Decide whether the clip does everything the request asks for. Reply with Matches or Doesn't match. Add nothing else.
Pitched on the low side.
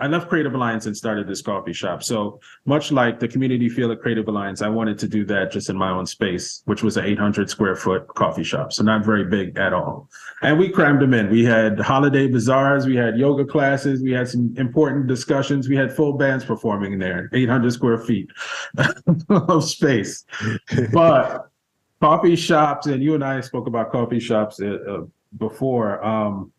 Matches